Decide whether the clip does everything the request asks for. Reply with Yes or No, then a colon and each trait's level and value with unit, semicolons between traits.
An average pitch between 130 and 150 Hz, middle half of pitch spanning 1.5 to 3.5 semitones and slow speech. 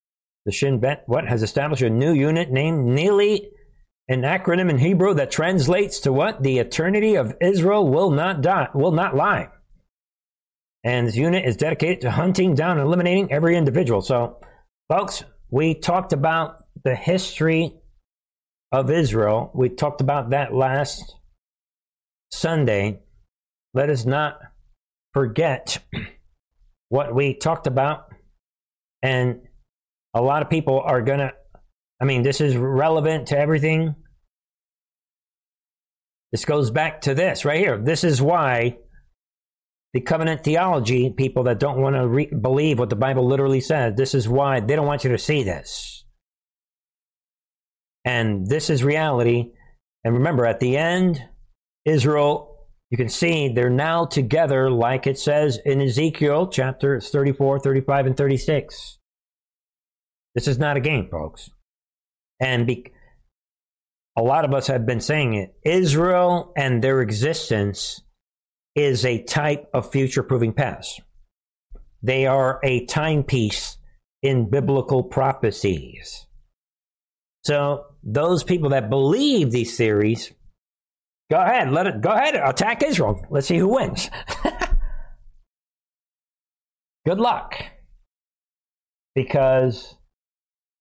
No: low, 135 Hz; average, 4.0 semitones; slow, 130 wpm